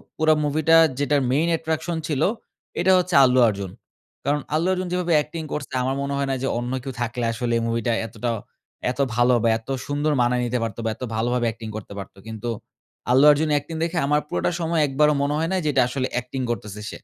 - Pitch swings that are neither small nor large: Yes, average, 4.5 semitones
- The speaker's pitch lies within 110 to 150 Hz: Yes, medium, 140 Hz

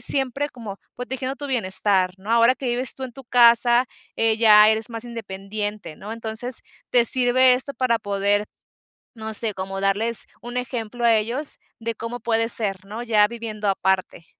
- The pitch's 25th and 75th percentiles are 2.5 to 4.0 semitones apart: Yes, average, 2.8 semitones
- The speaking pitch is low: No, high, 230 Hz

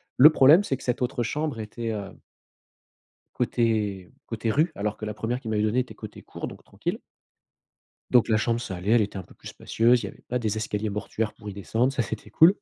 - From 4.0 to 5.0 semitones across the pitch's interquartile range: No, average, 2.8 semitones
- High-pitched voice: No, low, 115 Hz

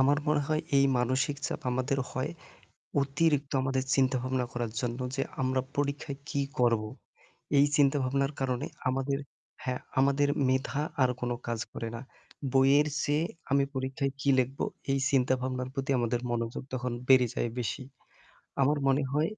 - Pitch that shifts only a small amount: Yes, narrow, 1.7 semitones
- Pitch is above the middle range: No, low, 135 Hz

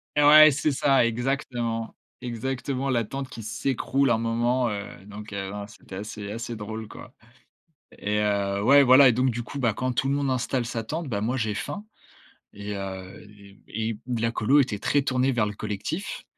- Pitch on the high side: No, low, 115 Hz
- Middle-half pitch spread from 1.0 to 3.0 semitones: No, average, 4.0 semitones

